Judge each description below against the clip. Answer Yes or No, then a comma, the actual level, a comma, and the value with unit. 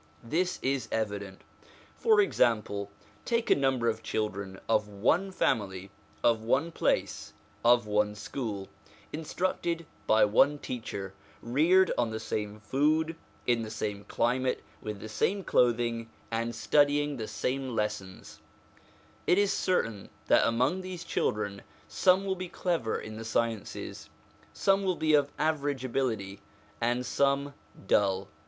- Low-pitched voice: Yes, low, 120 Hz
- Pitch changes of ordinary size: No, wide, 5.9 semitones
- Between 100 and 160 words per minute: Yes, slow, 135 wpm